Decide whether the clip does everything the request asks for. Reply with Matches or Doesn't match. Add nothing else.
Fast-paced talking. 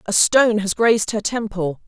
Doesn't match